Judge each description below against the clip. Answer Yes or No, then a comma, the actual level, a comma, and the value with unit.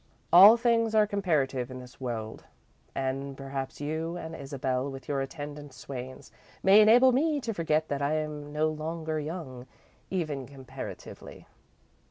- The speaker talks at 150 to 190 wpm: No, average, 140 wpm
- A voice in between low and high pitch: Yes, medium, 150 Hz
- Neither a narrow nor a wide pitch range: Yes, average, 4.5 semitones